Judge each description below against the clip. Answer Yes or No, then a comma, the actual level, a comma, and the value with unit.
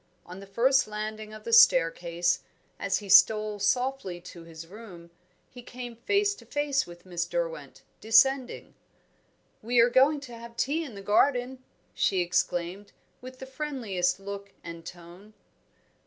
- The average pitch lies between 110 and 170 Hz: No, high, 215 Hz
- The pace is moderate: Yes, average, 150 wpm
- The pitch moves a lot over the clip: Yes, wide, 6.0 semitones